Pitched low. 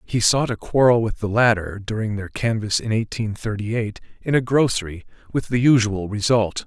Yes: low, 110 Hz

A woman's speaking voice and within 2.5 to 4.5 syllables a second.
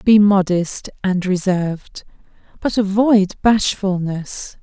Yes: female; 3.4 syllables/s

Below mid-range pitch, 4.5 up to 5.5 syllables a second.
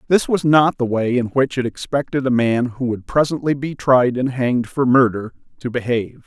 Yes: low, 130 Hz; 5.2 syllables/s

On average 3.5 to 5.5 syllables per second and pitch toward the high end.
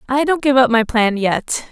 Yes: 4.6 syllables/s; high, 245 Hz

